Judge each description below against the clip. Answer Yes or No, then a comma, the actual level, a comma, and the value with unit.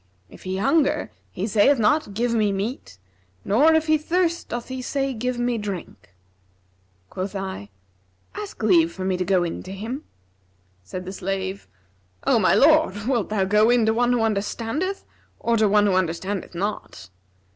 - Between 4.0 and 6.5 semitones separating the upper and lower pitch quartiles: Yes, average, 4.4 semitones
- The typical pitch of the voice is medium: No, high, 210 Hz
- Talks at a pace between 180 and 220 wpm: No, average, 170 wpm